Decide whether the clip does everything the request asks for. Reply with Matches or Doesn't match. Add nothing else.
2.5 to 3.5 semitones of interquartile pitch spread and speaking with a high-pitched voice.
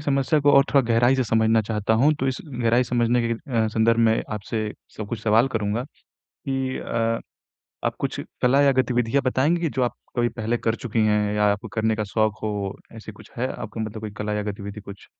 Doesn't match